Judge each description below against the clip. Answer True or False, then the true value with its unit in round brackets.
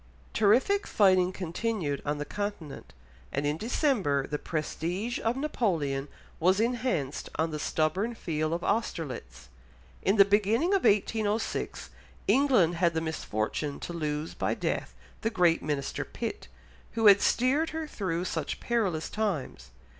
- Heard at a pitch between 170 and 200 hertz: True (185 Hz)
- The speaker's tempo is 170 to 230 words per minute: False (140 wpm)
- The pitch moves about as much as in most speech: False (6.6 semitones)